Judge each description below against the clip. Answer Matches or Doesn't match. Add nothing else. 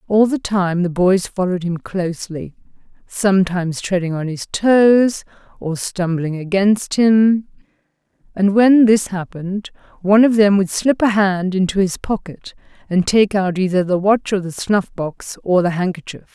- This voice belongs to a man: Doesn't match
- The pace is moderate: Matches